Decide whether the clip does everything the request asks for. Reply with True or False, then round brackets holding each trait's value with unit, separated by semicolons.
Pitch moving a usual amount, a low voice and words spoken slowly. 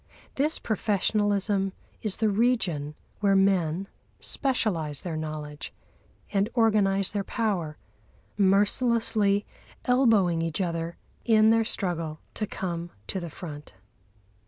False (4.5 semitones; 195 Hz; 110 wpm)